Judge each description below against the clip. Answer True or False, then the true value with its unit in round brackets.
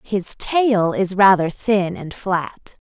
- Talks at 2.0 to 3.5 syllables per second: True (3.0 syllables/s)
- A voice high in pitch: True (195 Hz)